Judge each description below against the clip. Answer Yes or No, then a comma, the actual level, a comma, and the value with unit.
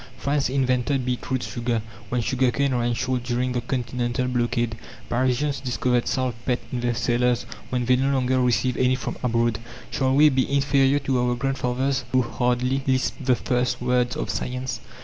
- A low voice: Yes, low, 125 Hz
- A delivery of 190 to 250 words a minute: No, average, 170 wpm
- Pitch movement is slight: Yes, narrow, 1.3 semitones